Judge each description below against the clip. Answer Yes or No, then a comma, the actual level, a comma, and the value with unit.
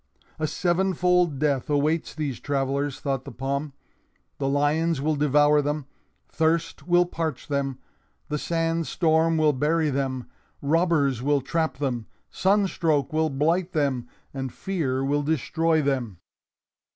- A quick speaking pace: No, slow, 135 wpm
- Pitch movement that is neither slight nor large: Yes, average, 3.1 semitones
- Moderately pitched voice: Yes, medium, 150 Hz